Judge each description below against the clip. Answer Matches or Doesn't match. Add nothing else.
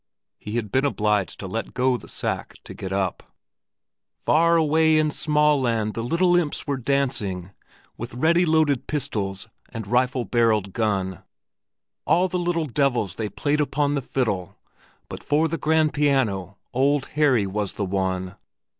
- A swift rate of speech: Doesn't match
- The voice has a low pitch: Matches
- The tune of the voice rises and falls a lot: Matches